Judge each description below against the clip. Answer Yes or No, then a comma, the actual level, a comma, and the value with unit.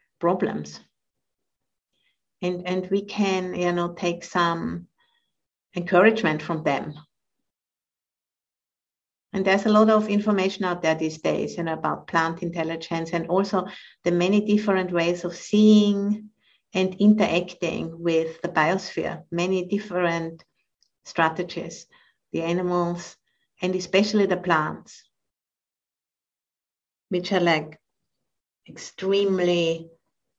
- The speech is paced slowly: Yes, slow, 105 wpm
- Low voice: No, medium, 175 Hz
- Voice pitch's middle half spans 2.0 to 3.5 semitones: Yes, narrow, 2.6 semitones